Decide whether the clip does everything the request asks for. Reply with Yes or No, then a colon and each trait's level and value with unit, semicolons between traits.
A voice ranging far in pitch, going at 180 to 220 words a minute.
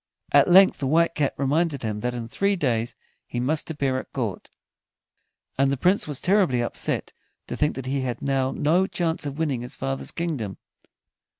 No: average, 4.6 semitones; average, 185 wpm